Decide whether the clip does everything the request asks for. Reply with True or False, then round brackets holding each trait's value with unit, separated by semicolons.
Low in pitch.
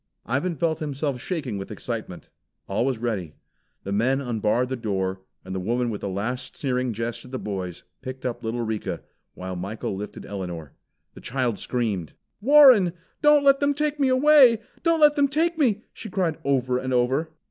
True (125 Hz)